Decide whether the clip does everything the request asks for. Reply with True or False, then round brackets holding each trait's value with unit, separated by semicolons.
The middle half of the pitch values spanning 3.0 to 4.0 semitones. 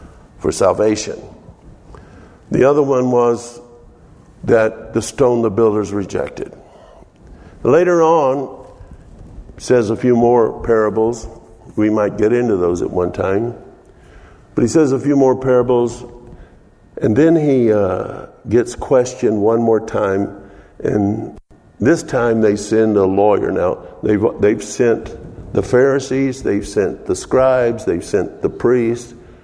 True (3.3 semitones)